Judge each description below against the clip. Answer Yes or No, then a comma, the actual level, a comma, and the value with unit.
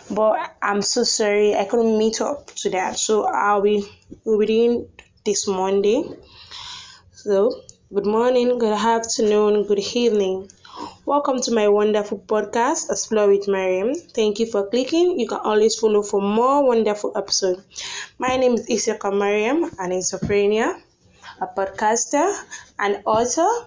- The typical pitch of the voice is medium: No, high, 215 Hz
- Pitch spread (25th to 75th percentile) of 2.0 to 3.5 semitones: Yes, average, 3.2 semitones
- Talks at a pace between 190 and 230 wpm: No, slow, 135 wpm